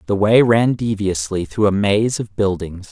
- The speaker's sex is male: Yes, male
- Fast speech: No, average, 185 wpm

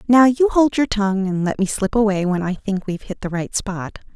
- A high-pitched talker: Yes, high, 205 Hz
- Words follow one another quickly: Yes, fast, 260 wpm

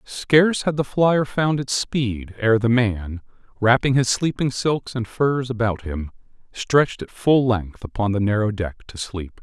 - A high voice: No, low, 120 Hz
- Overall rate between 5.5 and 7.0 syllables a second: No, 4.2 syllables/s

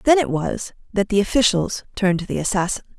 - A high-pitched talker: Yes, high, 205 Hz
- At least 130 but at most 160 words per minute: No, average, 200 wpm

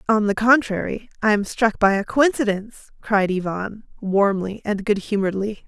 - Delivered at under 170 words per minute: Yes, average, 160 wpm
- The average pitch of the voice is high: Yes, high, 210 Hz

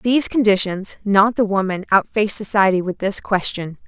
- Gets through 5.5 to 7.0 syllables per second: No, 5.3 syllables/s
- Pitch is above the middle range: Yes, high, 200 Hz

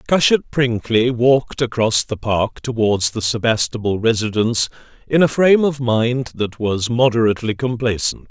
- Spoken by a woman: No, male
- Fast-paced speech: No, slow, 135 wpm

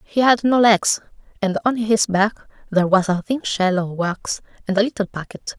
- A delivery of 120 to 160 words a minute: No, fast, 205 wpm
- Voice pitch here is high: Yes, high, 205 Hz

